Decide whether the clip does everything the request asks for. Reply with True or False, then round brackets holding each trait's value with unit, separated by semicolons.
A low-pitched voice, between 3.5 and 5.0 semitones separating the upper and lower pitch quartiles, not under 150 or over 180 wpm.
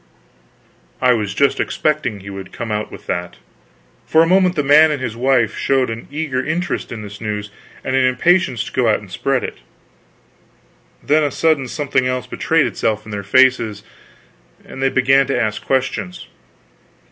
True (130 Hz; 4.7 semitones; 175 wpm)